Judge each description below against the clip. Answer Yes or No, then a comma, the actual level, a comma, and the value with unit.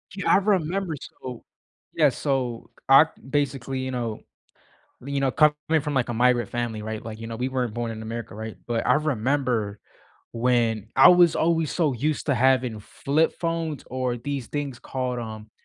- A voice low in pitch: Yes, low, 130 Hz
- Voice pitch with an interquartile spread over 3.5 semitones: Yes, average, 4.0 semitones